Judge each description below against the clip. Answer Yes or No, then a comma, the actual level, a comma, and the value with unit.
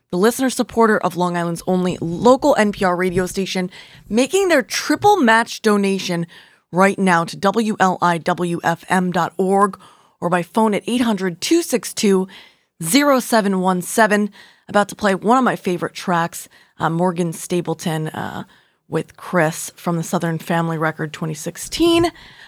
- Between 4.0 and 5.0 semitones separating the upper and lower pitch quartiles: Yes, average, 4.5 semitones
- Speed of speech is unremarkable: No, slow, 125 wpm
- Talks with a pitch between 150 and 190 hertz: Yes, medium, 185 Hz